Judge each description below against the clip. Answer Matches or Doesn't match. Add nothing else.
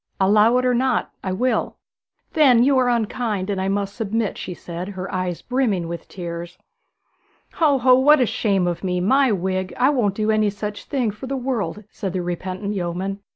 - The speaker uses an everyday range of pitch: Matches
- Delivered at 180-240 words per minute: Matches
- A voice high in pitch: Matches